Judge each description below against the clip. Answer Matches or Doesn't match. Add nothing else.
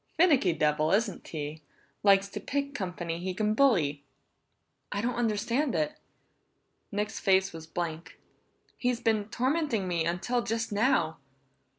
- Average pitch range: Doesn't match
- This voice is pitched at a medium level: Doesn't match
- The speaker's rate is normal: Doesn't match